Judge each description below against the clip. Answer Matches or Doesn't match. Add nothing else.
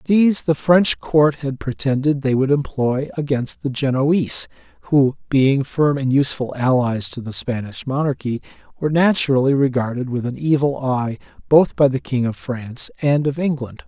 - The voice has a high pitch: Doesn't match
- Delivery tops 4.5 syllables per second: Matches